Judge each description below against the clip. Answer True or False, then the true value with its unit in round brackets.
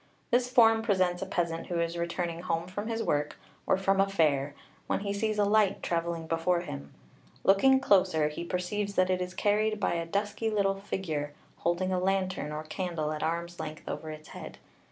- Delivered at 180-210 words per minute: True (195 wpm)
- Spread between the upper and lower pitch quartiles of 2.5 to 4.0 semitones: True (3.3 semitones)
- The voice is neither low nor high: True (180 Hz)